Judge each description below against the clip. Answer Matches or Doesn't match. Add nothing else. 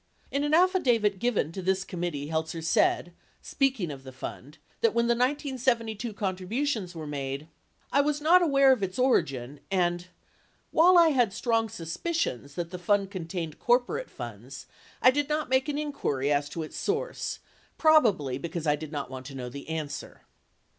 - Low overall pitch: Doesn't match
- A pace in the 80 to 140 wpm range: Doesn't match